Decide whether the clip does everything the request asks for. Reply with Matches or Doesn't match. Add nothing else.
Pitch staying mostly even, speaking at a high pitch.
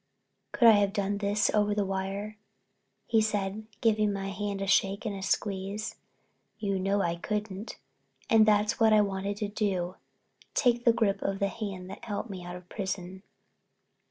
Matches